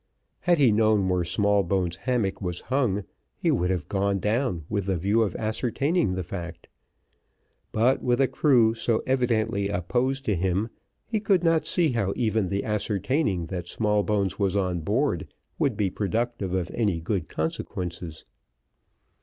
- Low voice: Yes, low, 105 Hz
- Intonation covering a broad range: No, average, 4.7 semitones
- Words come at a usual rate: Yes, average, 155 wpm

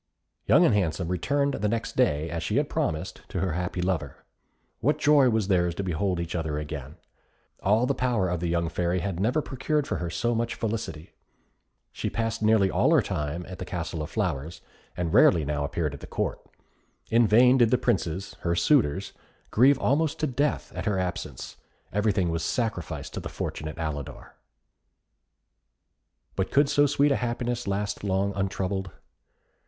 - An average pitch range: No, wide, 5.8 semitones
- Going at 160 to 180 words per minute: Yes, average, 175 wpm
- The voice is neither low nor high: No, very low, 95 Hz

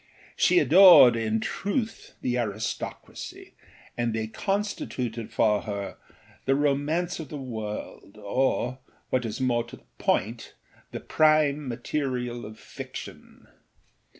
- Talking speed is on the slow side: Yes, slow, 120 wpm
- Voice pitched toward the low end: Yes, low, 125 Hz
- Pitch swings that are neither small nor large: Yes, average, 5.0 semitones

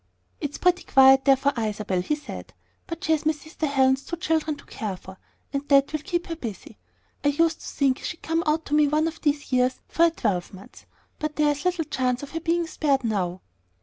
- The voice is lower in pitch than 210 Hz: No, very high, 290 Hz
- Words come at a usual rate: No, fast, 215 wpm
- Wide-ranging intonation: No, average, 3.7 semitones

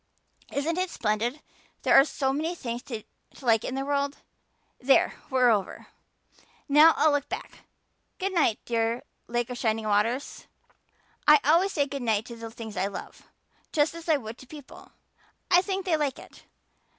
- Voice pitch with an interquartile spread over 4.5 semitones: Yes, average, 4.9 semitones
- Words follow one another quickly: No, average, 170 wpm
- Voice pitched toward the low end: No, very high, 270 Hz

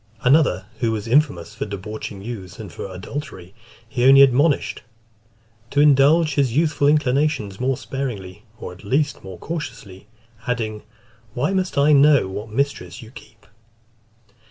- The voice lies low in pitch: Yes, low, 125 Hz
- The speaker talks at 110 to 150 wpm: Yes, average, 140 wpm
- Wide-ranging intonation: Yes, wide, 5.8 semitones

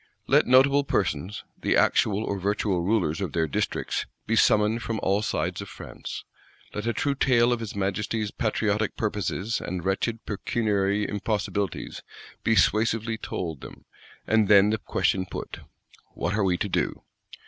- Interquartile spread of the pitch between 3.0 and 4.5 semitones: No, narrow, 2.5 semitones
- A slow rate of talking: No, average, 160 wpm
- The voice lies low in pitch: Yes, low, 105 Hz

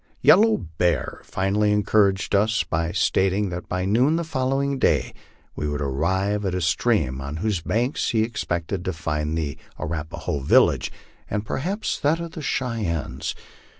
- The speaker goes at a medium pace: Yes, average, 155 wpm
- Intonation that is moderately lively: No, wide, 6.2 semitones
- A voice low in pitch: Yes, very low, 95 Hz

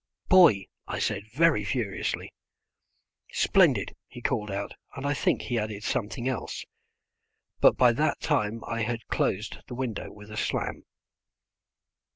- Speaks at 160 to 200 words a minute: No, average, 140 wpm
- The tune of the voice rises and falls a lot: No, average, 3.8 semitones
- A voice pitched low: Yes, low, 115 Hz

